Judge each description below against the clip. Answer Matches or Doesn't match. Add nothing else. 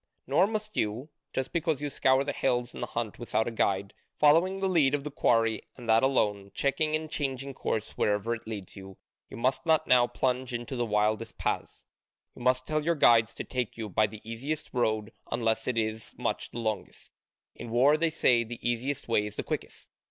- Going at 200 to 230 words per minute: Matches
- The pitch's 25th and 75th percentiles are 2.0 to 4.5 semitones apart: Matches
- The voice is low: Matches